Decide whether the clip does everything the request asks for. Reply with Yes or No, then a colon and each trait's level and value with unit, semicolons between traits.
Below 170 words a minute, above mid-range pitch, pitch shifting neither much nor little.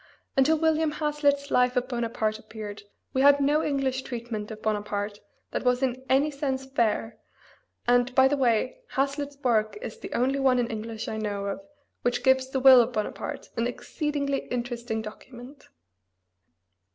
Yes: average, 160 wpm; very high, 250 Hz; average, 3.5 semitones